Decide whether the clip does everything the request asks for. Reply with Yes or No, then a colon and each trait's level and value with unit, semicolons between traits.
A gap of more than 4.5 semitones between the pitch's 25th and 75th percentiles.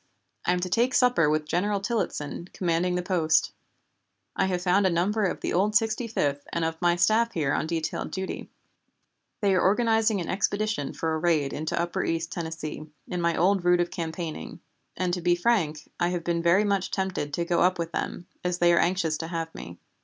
No: average, 2.9 semitones